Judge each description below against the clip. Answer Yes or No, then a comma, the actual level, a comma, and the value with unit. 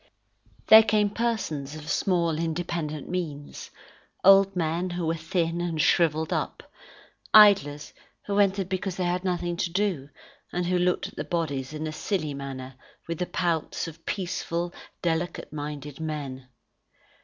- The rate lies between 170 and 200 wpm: No, average, 145 wpm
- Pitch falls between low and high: Yes, medium, 170 Hz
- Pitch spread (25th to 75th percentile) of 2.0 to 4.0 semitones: Yes, average, 3.0 semitones